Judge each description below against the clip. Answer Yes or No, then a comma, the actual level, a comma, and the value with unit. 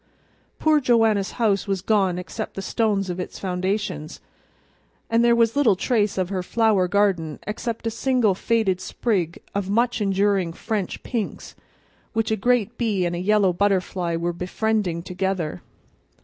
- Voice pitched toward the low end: No, high, 200 Hz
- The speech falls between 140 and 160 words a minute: Yes, average, 150 wpm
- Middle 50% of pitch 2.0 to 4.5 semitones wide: Yes, average, 3.6 semitones